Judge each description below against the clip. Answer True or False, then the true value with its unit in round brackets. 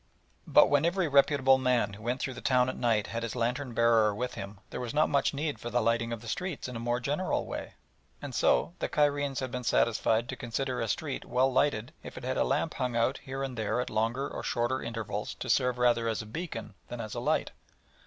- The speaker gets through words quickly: True (240 wpm)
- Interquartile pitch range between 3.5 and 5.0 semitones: False (2.8 semitones)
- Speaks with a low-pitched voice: True (125 Hz)